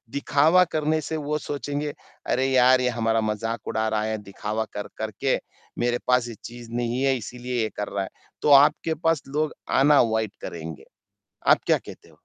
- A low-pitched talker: Yes, low, 120 Hz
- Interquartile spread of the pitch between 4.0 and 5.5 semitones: Yes, average, 4.5 semitones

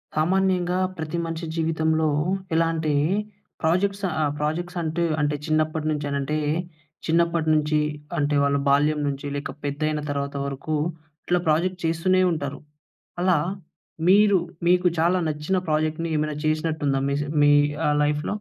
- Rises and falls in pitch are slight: Yes, narrow, 2.3 semitones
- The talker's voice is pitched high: No, medium, 155 Hz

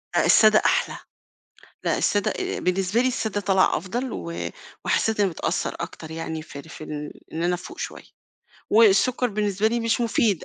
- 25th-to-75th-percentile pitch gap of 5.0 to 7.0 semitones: Yes, average, 5.3 semitones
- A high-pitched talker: Yes, high, 200 Hz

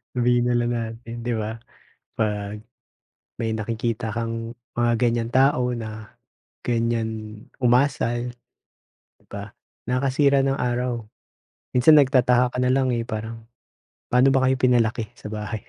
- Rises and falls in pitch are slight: Yes, narrow, 2.0 semitones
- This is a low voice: Yes, low, 120 Hz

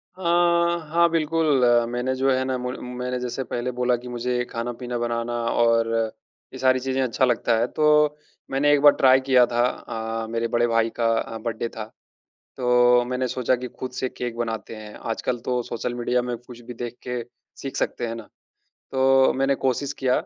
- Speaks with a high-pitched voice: No, low, 125 Hz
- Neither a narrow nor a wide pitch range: No, narrow, 1.7 semitones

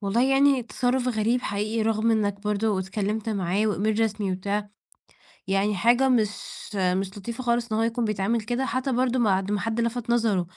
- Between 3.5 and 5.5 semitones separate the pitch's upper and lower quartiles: No, average, 2.8 semitones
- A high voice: Yes, high, 220 Hz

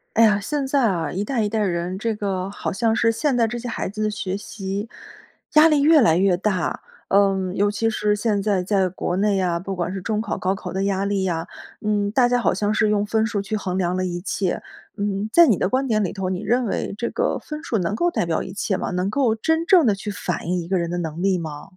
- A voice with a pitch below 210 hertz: Yes, high, 200 Hz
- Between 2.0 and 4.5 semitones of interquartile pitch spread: Yes, average, 3.3 semitones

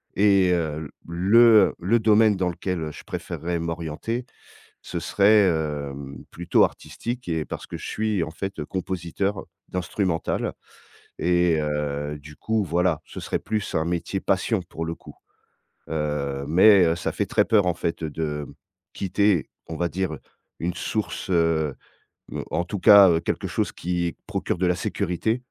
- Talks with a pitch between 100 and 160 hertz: No, very low, 85 Hz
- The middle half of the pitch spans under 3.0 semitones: No, average, 3.5 semitones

